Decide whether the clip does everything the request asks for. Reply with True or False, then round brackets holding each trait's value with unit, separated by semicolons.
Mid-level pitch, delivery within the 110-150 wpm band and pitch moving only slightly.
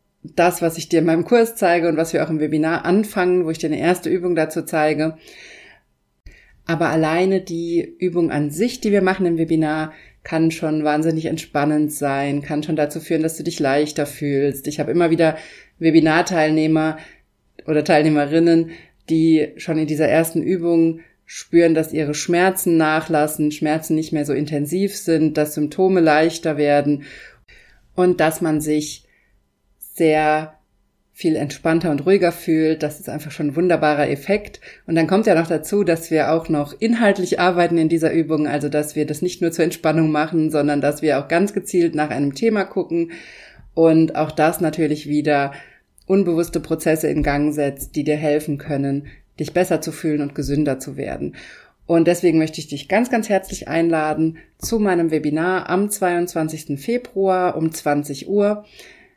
False (160 Hz; 170 wpm; 2.2 semitones)